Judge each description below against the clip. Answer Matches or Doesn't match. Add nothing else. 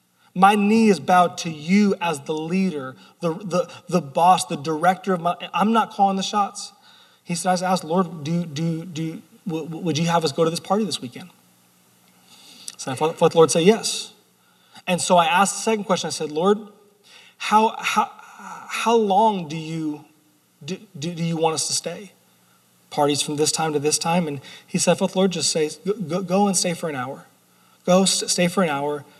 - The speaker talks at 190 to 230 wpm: Matches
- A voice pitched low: Doesn't match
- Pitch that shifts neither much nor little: Matches